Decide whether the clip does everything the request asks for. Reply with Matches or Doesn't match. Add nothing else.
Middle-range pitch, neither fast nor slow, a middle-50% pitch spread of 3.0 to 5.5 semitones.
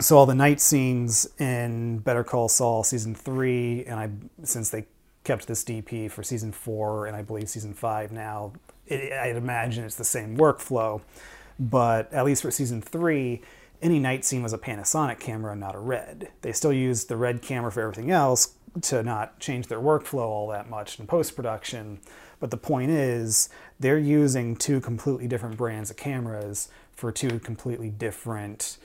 Doesn't match